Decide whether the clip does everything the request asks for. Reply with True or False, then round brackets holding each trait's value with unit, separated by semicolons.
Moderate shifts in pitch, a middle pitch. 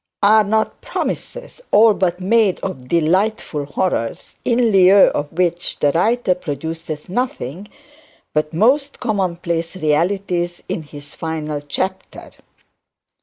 True (4.6 semitones; 180 Hz)